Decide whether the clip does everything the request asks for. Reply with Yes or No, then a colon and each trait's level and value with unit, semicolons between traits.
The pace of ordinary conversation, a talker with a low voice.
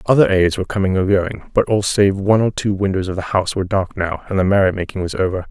No: fast, 260 wpm; very low, 95 Hz